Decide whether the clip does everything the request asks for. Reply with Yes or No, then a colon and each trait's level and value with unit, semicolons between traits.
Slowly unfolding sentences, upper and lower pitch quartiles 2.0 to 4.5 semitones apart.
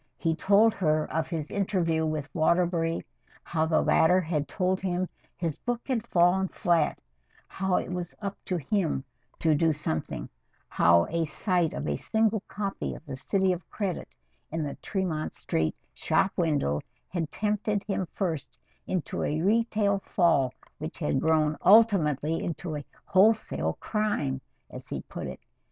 No: average, 155 wpm; average, 4.0 semitones